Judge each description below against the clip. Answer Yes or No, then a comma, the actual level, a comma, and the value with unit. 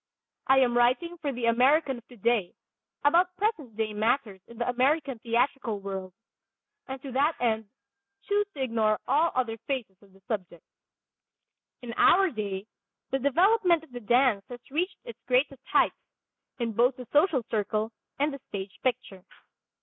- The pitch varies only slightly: No, average, 4.4 semitones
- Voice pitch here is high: Yes, high, 245 Hz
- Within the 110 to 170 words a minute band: Yes, average, 155 wpm